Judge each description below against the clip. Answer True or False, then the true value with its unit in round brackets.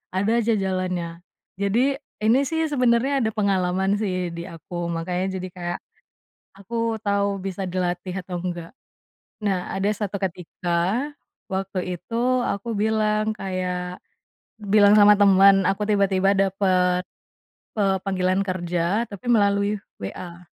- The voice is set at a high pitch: True (195 Hz)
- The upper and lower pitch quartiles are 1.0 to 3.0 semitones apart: True (2.6 semitones)